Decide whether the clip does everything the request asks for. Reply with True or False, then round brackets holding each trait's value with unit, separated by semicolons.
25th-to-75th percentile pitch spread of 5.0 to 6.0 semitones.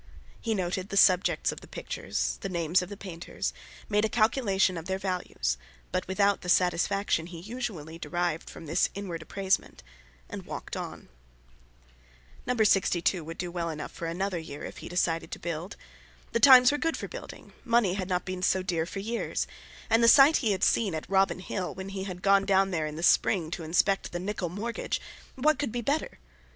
False (3.1 semitones)